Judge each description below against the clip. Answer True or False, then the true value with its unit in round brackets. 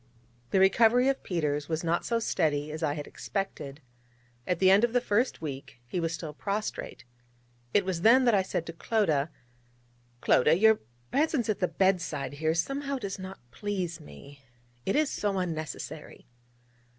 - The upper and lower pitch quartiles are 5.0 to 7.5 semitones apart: True (5.4 semitones)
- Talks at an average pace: True (170 wpm)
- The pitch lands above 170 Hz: True (185 Hz)